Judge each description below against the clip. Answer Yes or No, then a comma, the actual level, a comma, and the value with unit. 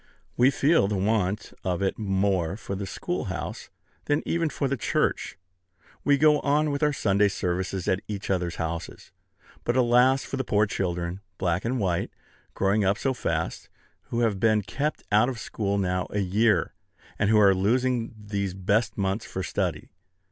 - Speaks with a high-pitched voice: No, low, 105 Hz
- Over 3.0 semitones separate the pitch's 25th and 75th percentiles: Yes, average, 4.3 semitones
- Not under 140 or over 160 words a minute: No, average, 170 wpm